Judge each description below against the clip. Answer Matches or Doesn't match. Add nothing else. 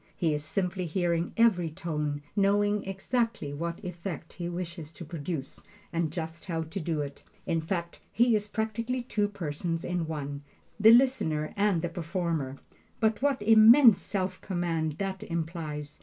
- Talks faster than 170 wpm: Doesn't match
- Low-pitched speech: Doesn't match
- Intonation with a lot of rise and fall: Doesn't match